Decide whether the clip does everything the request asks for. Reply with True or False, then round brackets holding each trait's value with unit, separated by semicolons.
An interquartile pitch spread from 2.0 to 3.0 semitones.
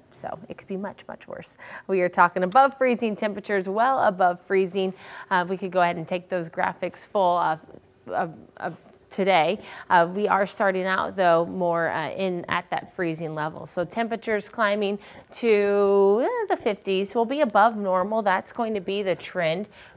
True (2.7 semitones)